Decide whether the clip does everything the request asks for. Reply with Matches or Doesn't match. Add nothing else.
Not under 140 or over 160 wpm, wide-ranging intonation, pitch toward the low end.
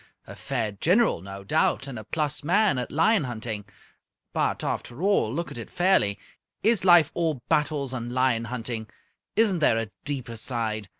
Doesn't match